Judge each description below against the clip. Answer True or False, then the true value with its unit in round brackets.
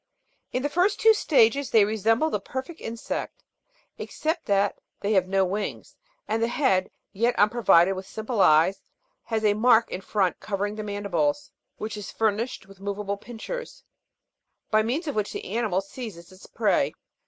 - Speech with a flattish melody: False (3.6 semitones)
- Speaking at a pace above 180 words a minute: False (170 wpm)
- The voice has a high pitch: True (215 Hz)